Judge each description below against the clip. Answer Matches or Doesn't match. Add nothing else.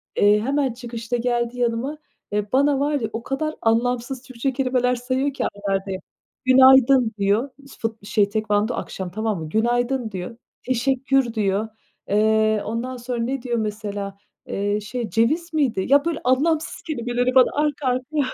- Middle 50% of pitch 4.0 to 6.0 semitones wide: Doesn't match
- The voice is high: Matches